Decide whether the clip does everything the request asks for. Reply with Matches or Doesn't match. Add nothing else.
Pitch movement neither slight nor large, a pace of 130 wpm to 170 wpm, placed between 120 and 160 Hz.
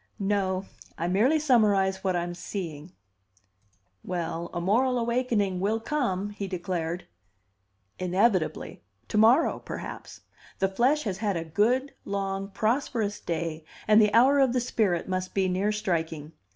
Doesn't match